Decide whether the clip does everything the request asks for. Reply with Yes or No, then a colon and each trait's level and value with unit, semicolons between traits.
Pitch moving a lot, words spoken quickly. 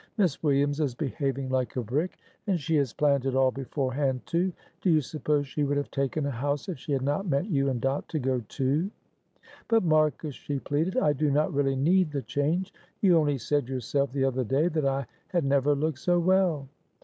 No: average, 2.7 semitones; fast, 210 wpm